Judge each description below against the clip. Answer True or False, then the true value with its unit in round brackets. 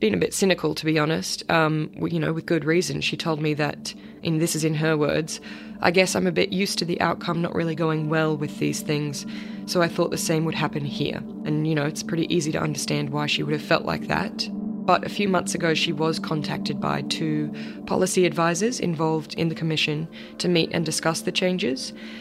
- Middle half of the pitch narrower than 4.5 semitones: True (2.7 semitones)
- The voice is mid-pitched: True (165 Hz)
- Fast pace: True (225 wpm)